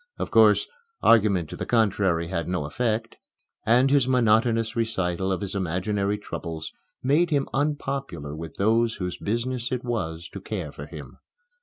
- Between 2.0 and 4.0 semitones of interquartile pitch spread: No, average, 5.0 semitones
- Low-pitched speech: Yes, low, 110 Hz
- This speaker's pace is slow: No, average, 155 wpm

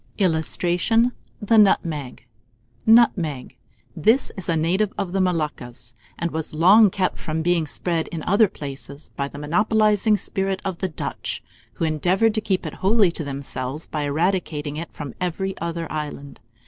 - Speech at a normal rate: Yes, average, 155 wpm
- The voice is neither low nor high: Yes, medium, 170 Hz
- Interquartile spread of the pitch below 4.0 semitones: No, average, 4.3 semitones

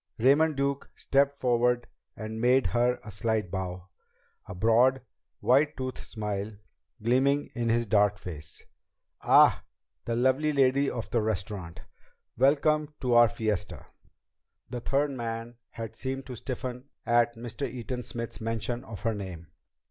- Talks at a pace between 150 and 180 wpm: No, average, 140 wpm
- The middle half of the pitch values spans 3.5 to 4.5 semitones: No, average, 3.1 semitones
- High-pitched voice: No, low, 120 Hz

